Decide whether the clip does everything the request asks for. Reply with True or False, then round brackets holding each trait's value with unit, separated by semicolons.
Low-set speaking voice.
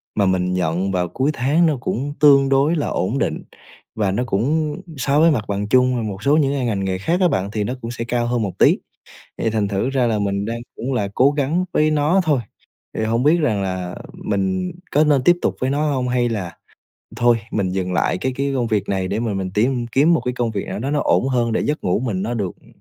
True (120 Hz)